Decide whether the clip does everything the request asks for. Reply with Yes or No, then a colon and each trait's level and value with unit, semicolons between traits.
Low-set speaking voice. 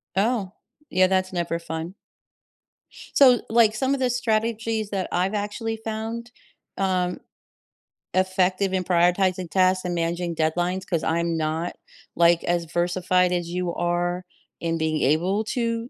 No: medium, 185 Hz